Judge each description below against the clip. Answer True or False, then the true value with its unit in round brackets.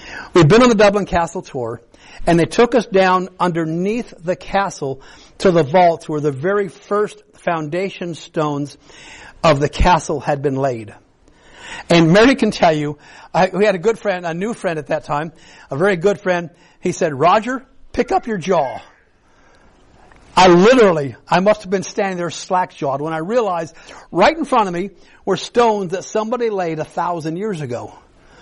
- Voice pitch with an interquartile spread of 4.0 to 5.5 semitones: True (4.6 semitones)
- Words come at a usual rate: True (180 wpm)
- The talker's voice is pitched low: False (180 Hz)